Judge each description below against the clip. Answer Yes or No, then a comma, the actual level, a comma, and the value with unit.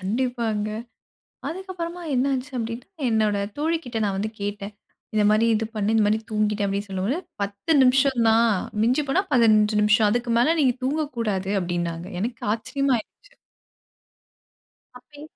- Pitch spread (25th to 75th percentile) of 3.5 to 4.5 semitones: Yes, average, 4.0 semitones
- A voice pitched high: Yes, high, 225 Hz